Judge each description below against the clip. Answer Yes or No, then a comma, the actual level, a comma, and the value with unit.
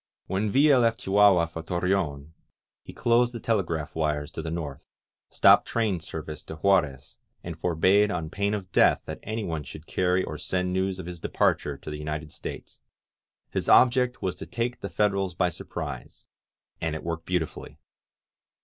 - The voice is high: No, very low, 90 Hz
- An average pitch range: Yes, average, 4.3 semitones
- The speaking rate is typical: Yes, average, 165 wpm